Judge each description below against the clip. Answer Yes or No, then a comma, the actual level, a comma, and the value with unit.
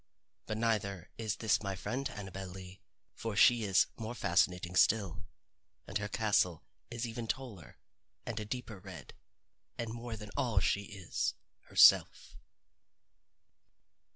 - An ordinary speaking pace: No, slow, 130 wpm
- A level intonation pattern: No, average, 3.3 semitones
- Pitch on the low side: Yes, low, 105 Hz